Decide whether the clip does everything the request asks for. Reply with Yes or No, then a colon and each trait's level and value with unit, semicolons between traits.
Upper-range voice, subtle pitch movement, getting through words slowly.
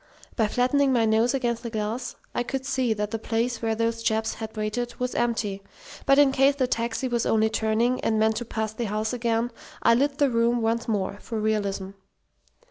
No: high, 230 Hz; narrow, 2.1 semitones; fast, 205 wpm